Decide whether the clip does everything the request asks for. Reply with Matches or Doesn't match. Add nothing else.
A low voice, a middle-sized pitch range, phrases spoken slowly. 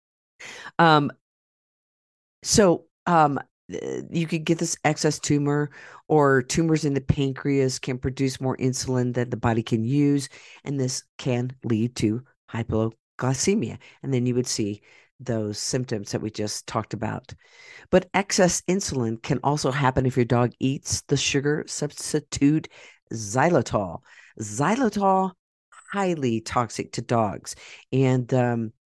Matches